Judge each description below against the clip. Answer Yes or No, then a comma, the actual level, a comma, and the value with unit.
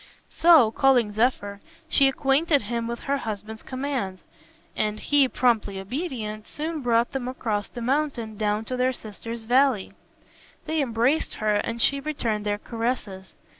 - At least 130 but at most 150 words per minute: Yes, average, 145 wpm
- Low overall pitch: No, high, 235 Hz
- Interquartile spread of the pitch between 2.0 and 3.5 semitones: No, average, 4.0 semitones